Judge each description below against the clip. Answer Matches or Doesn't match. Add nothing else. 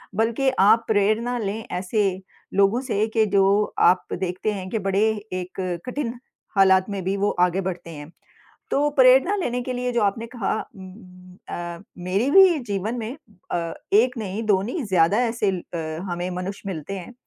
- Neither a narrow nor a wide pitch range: Matches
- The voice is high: Matches